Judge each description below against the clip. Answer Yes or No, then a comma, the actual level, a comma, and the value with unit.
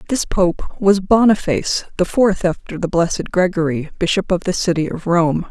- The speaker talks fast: No, average, 175 wpm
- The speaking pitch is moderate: Yes, medium, 180 Hz